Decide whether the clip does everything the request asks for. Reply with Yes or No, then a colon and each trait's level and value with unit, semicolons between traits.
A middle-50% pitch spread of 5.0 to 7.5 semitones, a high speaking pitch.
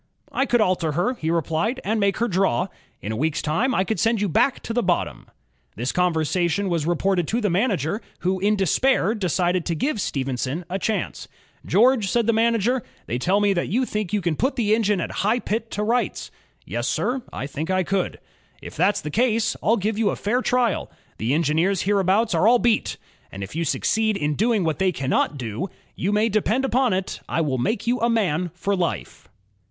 Yes: average, 5.3 semitones; high, 195 Hz